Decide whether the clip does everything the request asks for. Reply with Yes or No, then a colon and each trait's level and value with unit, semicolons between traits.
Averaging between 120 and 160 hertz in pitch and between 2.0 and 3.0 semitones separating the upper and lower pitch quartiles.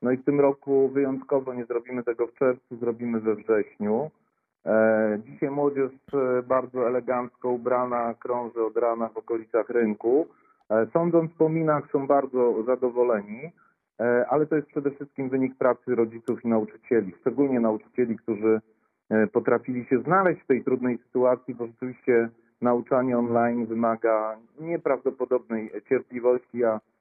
Yes: low, 125 Hz; narrow, 2.4 semitones